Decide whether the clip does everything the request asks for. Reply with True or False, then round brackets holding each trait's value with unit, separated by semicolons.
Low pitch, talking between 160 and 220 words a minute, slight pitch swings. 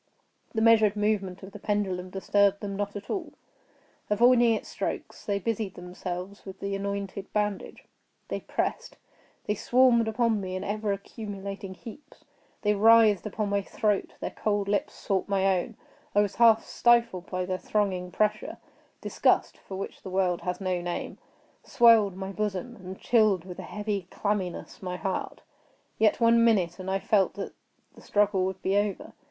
False (200 Hz; 165 wpm; 2.2 semitones)